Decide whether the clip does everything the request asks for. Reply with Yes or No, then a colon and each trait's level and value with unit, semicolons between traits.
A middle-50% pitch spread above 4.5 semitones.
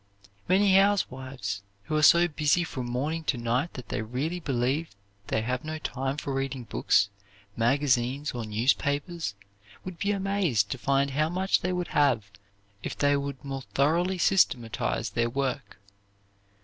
Yes: average, 5.1 semitones